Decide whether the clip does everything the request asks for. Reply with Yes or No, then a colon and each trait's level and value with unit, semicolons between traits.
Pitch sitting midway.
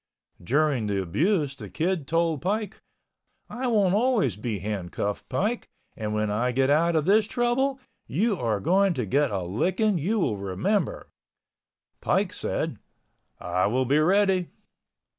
Yes: medium, 155 Hz